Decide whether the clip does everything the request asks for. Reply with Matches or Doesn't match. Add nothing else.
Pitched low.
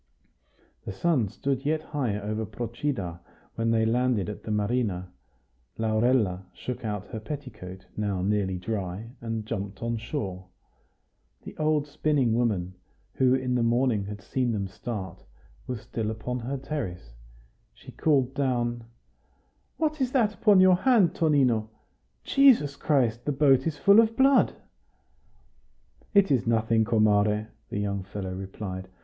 Matches